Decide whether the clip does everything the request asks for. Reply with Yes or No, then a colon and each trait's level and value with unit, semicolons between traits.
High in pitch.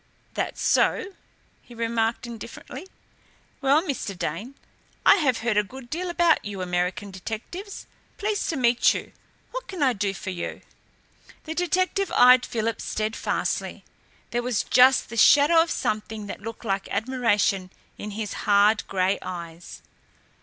Yes: high, 230 Hz